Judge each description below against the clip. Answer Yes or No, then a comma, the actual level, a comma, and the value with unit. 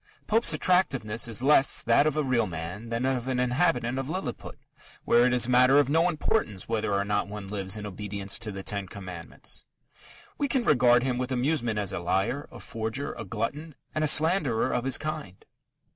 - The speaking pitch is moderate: No, low, 120 Hz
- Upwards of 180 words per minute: Yes, average, 200 wpm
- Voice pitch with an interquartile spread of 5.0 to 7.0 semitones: Yes, wide, 5.5 semitones